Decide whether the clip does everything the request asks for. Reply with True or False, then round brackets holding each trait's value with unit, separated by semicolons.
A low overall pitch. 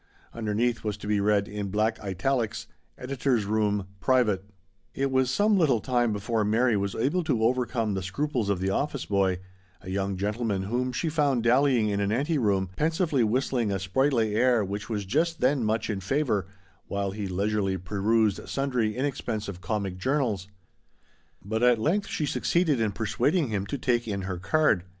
True (110 Hz)